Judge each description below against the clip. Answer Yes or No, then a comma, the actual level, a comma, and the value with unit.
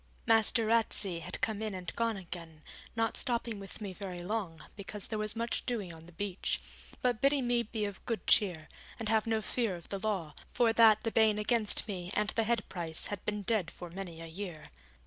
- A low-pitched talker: No, high, 210 Hz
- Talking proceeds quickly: Yes, fast, 210 wpm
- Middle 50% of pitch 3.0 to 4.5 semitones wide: Yes, average, 3.9 semitones